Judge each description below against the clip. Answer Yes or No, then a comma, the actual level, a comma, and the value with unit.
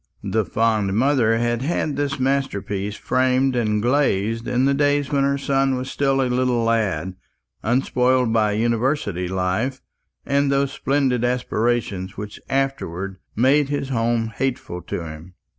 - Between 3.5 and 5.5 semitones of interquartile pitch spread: Yes, average, 4.1 semitones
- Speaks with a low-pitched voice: Yes, low, 125 Hz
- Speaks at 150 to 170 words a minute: No, average, 140 wpm